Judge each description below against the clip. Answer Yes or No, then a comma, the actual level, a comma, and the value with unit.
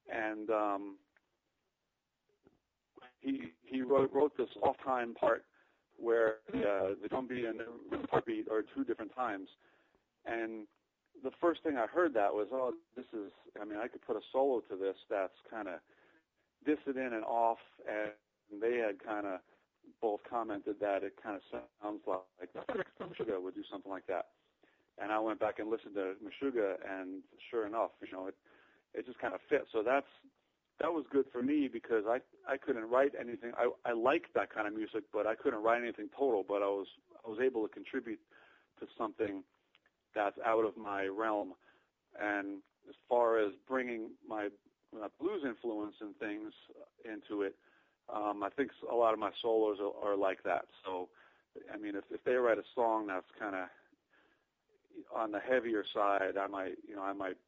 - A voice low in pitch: Yes, low, 115 Hz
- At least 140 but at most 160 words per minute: No, average, 180 wpm